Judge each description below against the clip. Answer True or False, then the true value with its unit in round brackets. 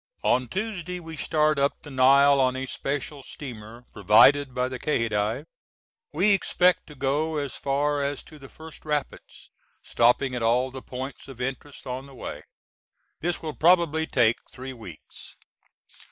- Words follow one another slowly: False (155 wpm)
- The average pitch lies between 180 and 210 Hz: False (140 Hz)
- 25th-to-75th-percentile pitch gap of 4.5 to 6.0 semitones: False (3.2 semitones)